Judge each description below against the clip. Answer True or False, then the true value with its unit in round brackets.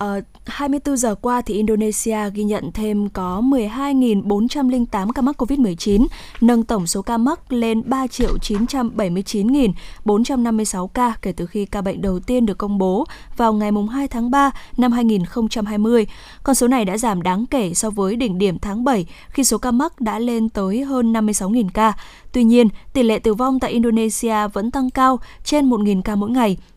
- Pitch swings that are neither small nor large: True (3.2 semitones)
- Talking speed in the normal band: True (175 wpm)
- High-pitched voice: True (225 Hz)